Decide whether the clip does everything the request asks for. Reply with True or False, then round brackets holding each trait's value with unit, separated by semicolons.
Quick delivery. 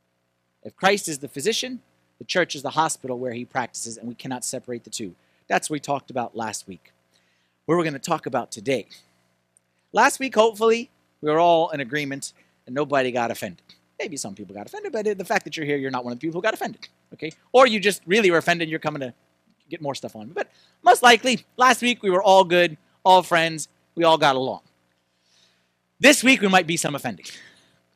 True (215 wpm)